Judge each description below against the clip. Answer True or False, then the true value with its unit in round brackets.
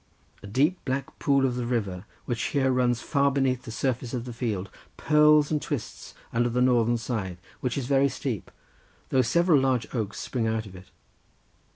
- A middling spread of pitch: True (3.1 semitones)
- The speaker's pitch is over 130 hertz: False (125 Hz)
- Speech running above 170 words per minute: True (185 wpm)